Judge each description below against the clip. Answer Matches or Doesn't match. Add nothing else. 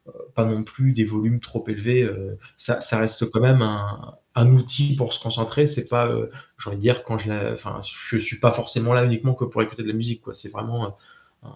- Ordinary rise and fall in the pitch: Doesn't match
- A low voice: Matches